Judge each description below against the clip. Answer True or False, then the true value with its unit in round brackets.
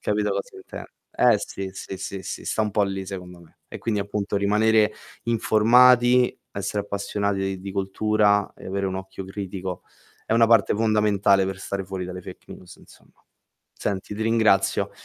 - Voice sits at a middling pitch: False (100 Hz)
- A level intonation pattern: True (1.9 semitones)